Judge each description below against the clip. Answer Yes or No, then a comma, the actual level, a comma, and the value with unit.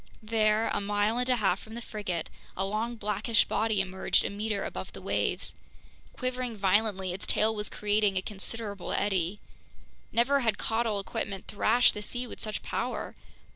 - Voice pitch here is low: No, high, 210 Hz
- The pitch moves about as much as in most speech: No, narrow, 2.2 semitones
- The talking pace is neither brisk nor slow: Yes, average, 170 wpm